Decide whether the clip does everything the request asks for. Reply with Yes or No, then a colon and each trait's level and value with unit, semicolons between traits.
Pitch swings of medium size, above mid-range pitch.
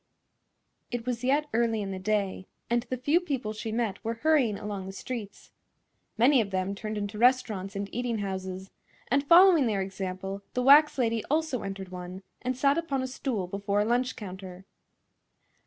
Yes: average, 4.7 semitones; high, 220 Hz